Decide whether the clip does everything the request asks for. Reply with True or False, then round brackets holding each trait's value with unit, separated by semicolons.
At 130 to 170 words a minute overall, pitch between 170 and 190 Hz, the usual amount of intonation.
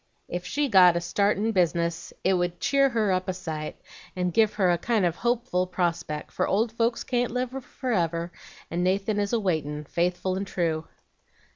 False (190 wpm; 185 Hz; 4.4 semitones)